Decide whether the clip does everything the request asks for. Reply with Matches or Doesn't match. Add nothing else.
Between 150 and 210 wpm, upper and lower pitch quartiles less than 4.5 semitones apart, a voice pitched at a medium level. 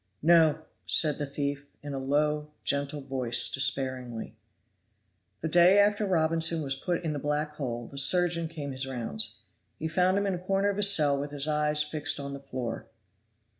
Matches